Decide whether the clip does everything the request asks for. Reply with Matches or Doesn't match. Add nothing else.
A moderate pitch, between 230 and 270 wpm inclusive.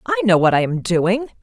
Doesn't match